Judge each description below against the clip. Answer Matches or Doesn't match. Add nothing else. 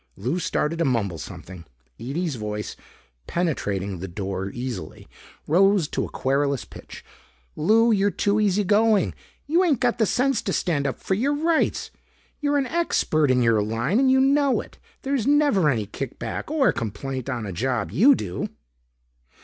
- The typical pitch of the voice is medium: Matches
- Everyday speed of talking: Matches